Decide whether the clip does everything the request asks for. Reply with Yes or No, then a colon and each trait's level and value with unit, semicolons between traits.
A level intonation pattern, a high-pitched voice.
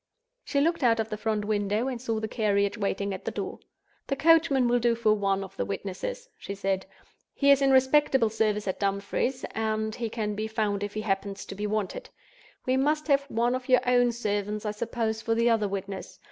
No: average, 3.5 semitones; high, 220 Hz